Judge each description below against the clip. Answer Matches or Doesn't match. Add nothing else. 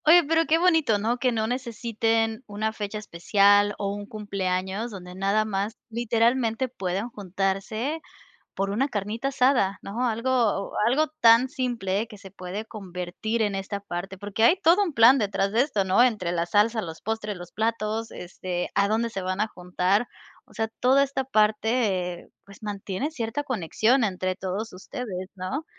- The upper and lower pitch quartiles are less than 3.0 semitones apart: Doesn't match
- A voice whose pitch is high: Matches